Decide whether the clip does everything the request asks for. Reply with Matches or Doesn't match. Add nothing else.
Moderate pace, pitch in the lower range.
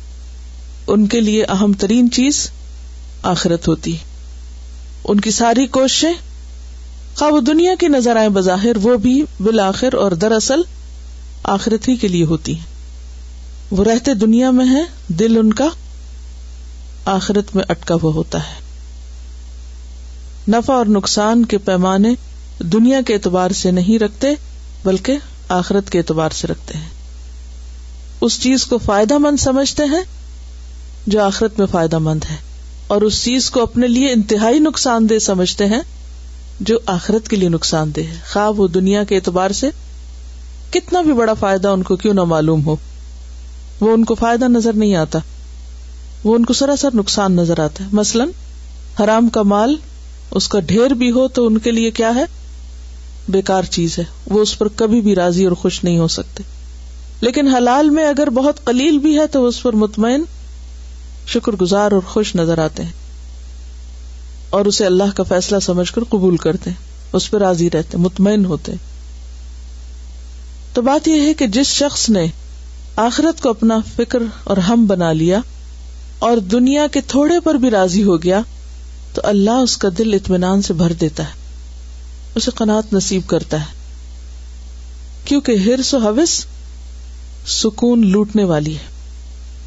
Doesn't match